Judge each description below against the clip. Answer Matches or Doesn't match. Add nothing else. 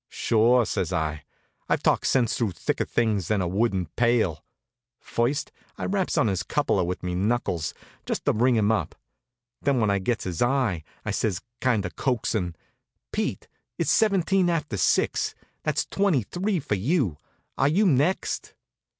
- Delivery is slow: Doesn't match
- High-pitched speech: Doesn't match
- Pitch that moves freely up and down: Matches